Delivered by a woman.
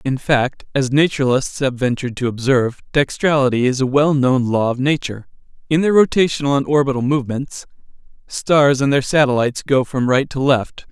No: male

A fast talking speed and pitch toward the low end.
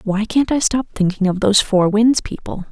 No: fast, 220 wpm; high, 210 Hz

